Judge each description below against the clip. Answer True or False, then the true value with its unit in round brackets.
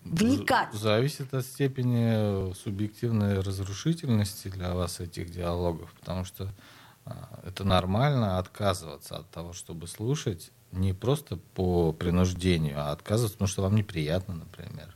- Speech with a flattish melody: False (4.8 semitones)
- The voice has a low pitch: True (100 Hz)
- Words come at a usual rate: True (120 wpm)